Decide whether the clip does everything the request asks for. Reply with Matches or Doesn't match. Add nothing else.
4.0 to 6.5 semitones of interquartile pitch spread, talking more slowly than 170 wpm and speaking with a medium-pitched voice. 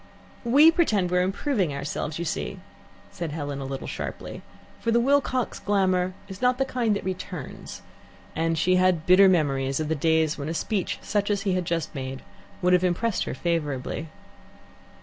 Doesn't match